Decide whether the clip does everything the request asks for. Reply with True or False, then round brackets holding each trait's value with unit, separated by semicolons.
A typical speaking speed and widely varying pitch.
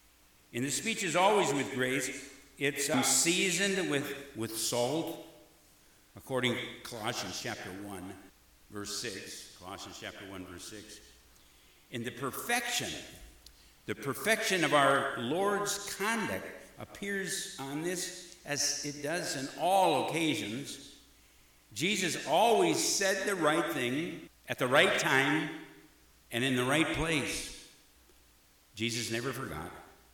False (120 wpm; 8.3 semitones)